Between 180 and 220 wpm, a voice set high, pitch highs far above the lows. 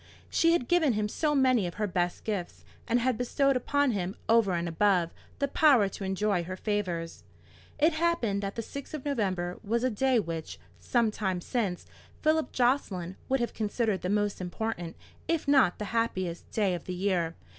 Yes: average, 185 wpm; high, 210 Hz; wide, 5.8 semitones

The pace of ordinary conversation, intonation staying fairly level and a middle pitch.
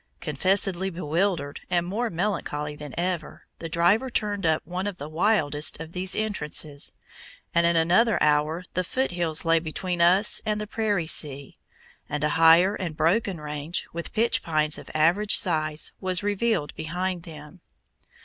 No: average, 160 wpm; average, 3.8 semitones; medium, 170 Hz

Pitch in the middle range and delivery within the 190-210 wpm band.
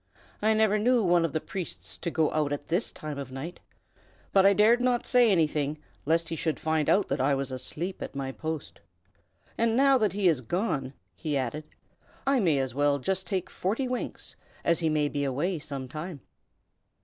Yes: medium, 160 Hz; average, 195 wpm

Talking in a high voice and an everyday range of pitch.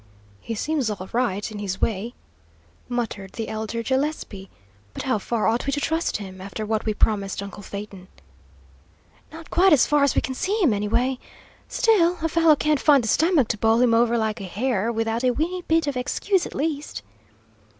No: high, 235 Hz; wide, 5.9 semitones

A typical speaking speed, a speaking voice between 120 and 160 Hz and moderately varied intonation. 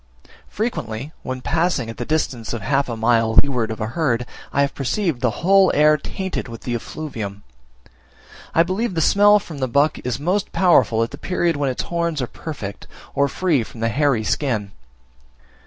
No: average, 190 wpm; medium, 140 Hz; wide, 6.3 semitones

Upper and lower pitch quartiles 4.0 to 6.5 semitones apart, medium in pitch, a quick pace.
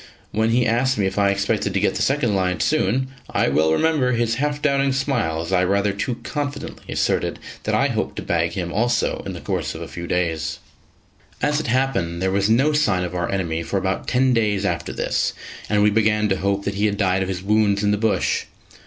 No: average, 4.7 semitones; low, 105 Hz; fast, 225 wpm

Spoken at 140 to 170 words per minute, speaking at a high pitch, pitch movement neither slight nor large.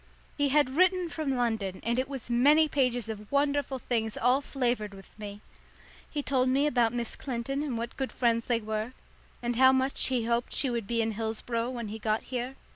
No: average, 200 wpm; high, 245 Hz; average, 3.1 semitones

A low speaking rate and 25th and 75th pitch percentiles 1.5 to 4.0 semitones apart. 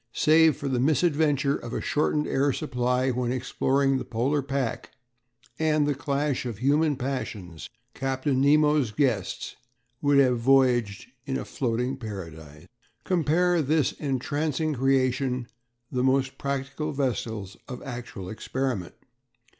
Yes: slow, 130 wpm; average, 2.9 semitones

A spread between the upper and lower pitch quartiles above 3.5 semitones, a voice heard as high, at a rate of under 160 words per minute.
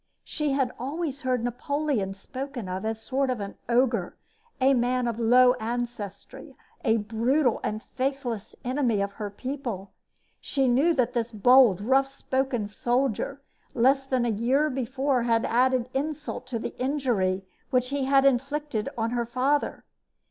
No: average, 3.1 semitones; very high, 250 Hz; average, 150 wpm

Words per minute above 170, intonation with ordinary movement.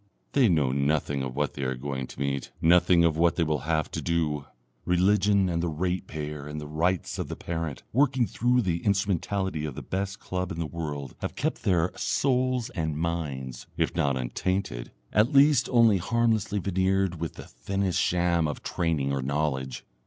Yes: average, 180 wpm; average, 4.6 semitones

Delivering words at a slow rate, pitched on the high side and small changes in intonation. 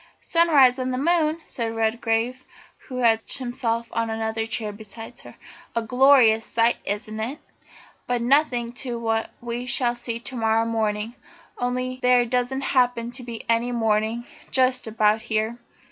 No: average, 155 wpm; high, 235 Hz; narrow, 2.1 semitones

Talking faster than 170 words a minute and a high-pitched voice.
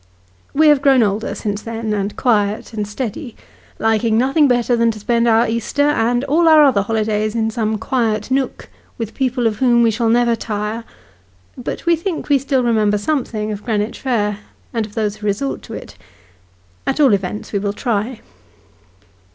Yes: average, 180 wpm; high, 230 Hz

